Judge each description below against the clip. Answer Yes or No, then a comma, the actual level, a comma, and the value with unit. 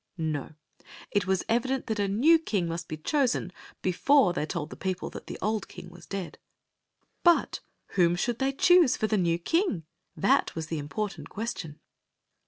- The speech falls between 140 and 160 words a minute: No, average, 180 wpm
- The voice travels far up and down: Yes, wide, 6.1 semitones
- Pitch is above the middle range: Yes, high, 195 Hz